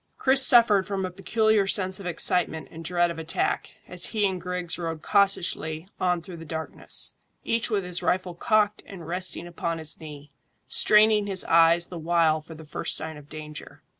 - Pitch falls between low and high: Yes, medium, 175 Hz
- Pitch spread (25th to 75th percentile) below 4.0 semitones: Yes, average, 3.3 semitones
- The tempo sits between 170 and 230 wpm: Yes, average, 185 wpm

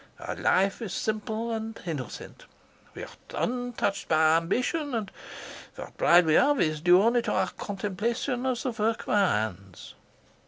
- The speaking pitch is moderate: No, high, 210 Hz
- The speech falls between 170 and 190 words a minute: No, average, 160 wpm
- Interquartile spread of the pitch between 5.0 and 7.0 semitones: Yes, wide, 5.4 semitones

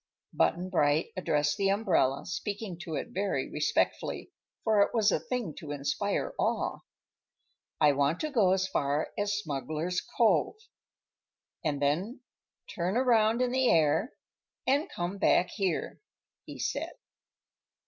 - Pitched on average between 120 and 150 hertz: No, medium, 185 Hz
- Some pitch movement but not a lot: No, wide, 6.1 semitones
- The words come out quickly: No, slow, 135 wpm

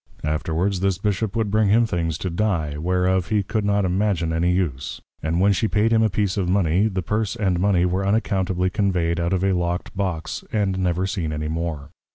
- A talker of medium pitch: No, very low, 95 Hz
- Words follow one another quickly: Yes, fast, 210 wpm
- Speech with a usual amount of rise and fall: Yes, average, 3.0 semitones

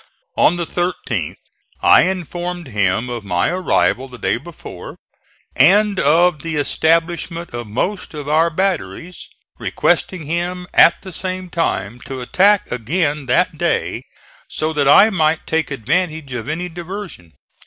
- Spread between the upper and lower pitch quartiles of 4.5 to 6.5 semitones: Yes, average, 5.0 semitones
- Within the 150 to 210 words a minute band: No, average, 140 wpm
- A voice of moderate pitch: Yes, medium, 165 Hz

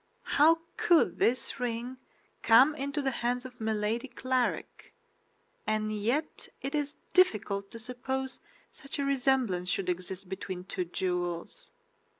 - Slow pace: Yes, slow, 130 wpm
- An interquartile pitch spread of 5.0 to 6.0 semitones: Yes, wide, 5.4 semitones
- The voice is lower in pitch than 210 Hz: No, high, 245 Hz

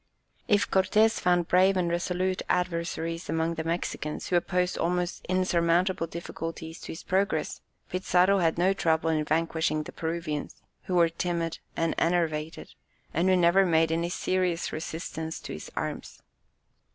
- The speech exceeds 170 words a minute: No, average, 145 wpm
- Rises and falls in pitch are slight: Yes, narrow, 1.9 semitones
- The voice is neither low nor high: Yes, medium, 170 Hz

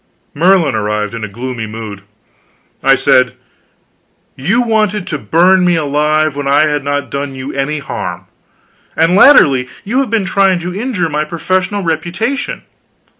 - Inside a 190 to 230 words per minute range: No, average, 150 wpm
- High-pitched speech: No, medium, 155 Hz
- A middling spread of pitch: No, wide, 5.7 semitones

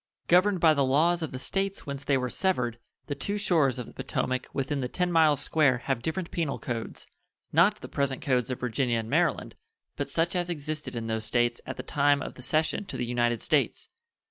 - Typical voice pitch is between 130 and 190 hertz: Yes, medium, 140 Hz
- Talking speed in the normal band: No, fast, 215 wpm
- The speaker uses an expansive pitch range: No, average, 4.8 semitones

